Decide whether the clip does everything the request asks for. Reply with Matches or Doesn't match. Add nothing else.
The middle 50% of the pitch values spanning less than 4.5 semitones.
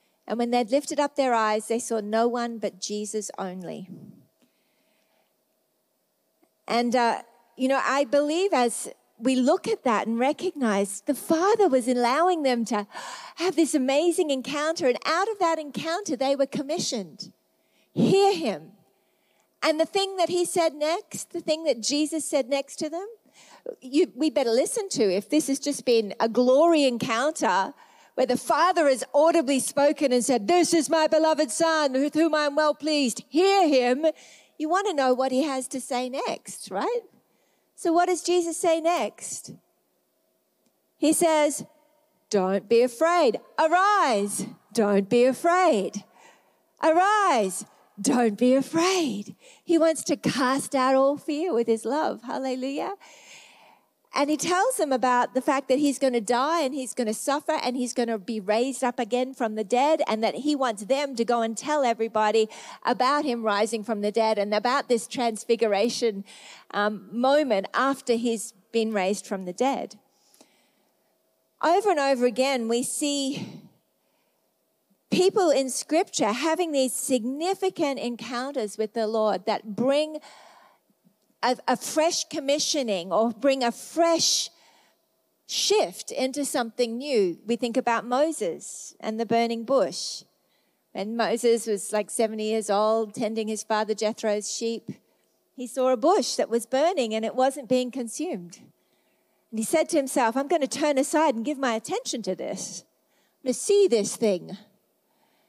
Doesn't match